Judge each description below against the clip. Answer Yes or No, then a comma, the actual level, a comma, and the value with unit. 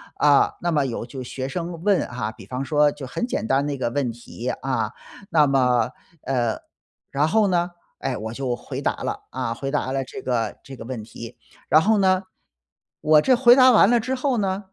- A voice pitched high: No, medium, 140 Hz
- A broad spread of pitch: Yes, wide, 6.8 semitones